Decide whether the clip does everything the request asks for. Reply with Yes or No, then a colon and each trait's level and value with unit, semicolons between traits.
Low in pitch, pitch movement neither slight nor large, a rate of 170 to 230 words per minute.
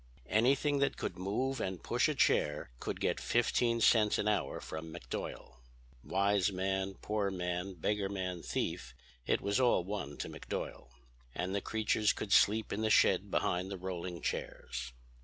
No: low, 100 Hz; average, 3.3 semitones; average, 160 wpm